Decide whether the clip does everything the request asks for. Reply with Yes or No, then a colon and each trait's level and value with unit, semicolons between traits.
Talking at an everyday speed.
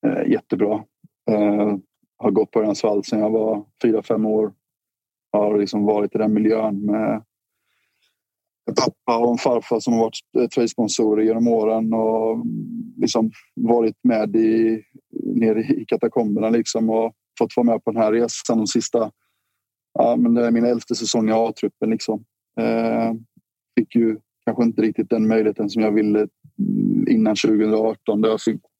Yes: average, 155 wpm